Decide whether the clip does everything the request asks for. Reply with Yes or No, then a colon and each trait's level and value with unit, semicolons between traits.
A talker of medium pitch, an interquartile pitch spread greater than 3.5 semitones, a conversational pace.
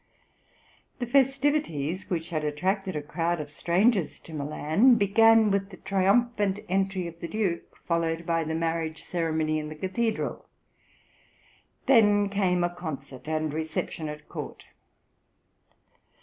No: medium, 175 Hz; average, 4.4 semitones; slow, 130 wpm